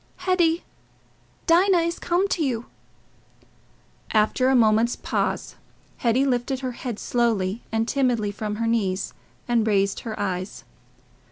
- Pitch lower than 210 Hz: No, high, 235 Hz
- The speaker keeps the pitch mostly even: No, average, 4.1 semitones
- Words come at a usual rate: No, slow, 125 wpm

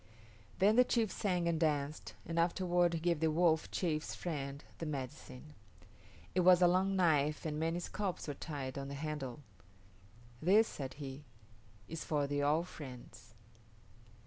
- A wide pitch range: No, average, 3.6 semitones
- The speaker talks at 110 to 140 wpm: No, average, 155 wpm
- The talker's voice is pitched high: No, medium, 155 Hz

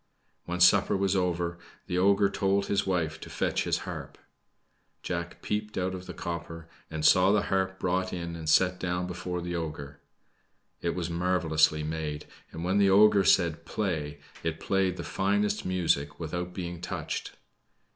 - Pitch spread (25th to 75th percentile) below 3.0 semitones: Yes, narrow, 2.4 semitones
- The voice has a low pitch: Yes, very low, 90 Hz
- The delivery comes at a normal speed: Yes, average, 165 wpm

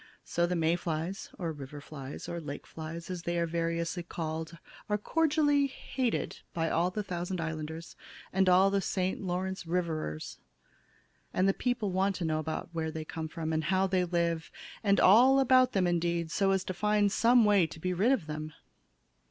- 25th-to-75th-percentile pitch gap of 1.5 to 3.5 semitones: Yes, average, 3.2 semitones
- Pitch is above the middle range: No, medium, 175 Hz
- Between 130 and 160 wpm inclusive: No, average, 190 wpm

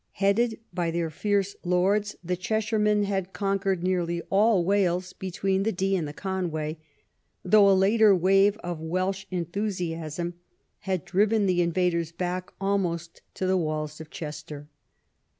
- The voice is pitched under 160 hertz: No, medium, 185 Hz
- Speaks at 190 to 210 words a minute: No, average, 140 wpm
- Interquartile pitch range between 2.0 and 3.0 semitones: Yes, narrow, 2.6 semitones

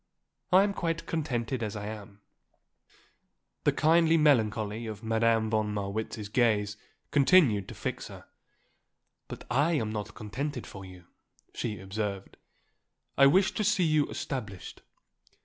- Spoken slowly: Yes, slow, 130 wpm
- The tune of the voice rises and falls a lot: Yes, wide, 6.2 semitones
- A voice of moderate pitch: No, low, 115 Hz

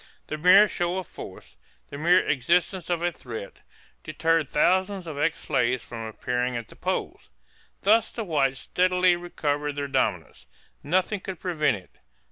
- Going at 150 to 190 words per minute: Yes, average, 155 wpm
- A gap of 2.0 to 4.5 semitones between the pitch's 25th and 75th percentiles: No, average, 5.0 semitones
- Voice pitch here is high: No, medium, 165 Hz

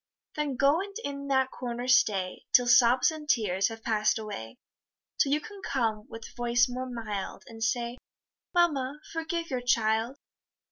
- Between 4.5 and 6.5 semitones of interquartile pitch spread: No, average, 3.9 semitones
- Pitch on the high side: Yes, high, 245 Hz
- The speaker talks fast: No, average, 155 wpm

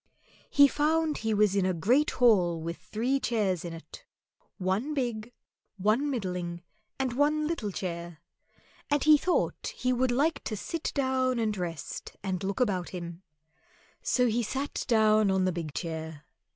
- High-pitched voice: Yes, high, 215 Hz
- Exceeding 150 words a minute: Yes, average, 160 wpm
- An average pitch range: No, wide, 6.4 semitones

